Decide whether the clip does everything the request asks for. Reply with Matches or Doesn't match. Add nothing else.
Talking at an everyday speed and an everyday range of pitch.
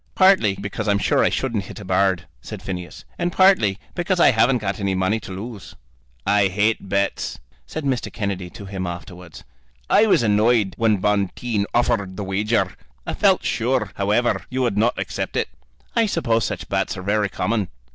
Matches